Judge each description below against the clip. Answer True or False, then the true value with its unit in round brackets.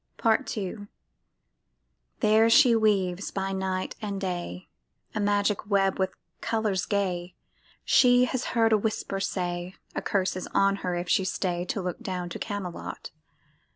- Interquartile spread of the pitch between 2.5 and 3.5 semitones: True (2.8 semitones)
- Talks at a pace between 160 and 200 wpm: False (150 wpm)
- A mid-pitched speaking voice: False (195 Hz)